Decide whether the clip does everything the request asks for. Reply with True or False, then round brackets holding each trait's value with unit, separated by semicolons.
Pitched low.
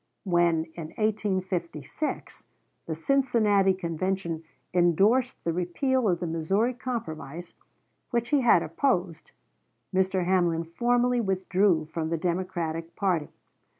False (185 Hz)